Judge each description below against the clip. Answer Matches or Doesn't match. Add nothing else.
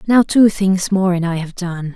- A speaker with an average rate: Doesn't match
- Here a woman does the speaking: Matches